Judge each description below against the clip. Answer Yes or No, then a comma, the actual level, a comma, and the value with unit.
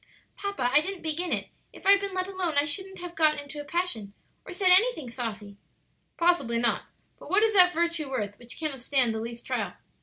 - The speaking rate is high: Yes, fast, 210 wpm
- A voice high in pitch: Yes, very high, 315 Hz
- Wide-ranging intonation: Yes, wide, 7.1 semitones